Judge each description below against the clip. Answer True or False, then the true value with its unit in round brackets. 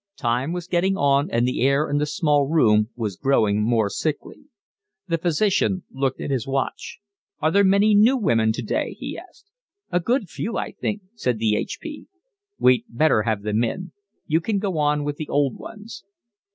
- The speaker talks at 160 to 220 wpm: True (180 wpm)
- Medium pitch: True (145 Hz)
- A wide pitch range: True (7.7 semitones)